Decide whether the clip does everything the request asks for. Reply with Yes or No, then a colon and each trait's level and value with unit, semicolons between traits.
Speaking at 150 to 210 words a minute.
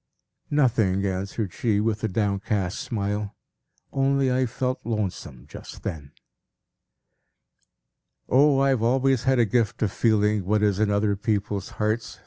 No: slow, 135 wpm